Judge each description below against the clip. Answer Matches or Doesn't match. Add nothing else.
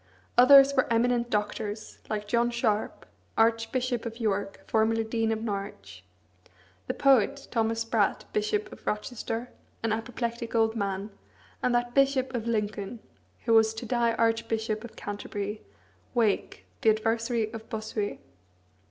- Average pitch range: Doesn't match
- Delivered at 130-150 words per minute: Matches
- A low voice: Doesn't match